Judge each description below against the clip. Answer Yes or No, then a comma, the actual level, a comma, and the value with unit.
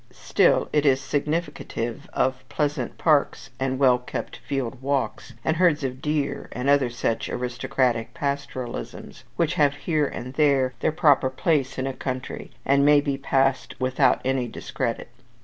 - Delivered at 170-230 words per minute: No, average, 150 wpm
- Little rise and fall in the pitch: Yes, narrow, 2.1 semitones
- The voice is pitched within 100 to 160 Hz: Yes, low, 135 Hz